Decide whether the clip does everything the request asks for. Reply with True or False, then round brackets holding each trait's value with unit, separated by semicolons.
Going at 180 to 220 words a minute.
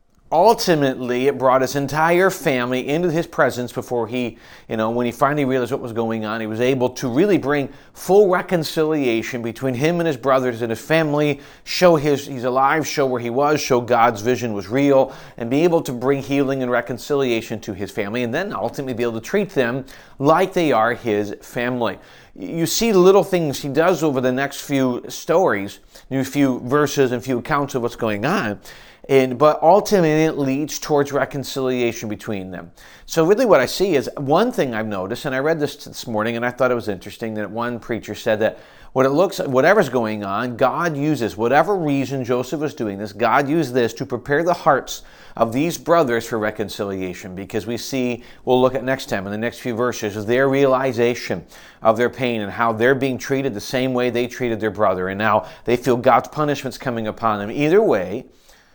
True (205 wpm)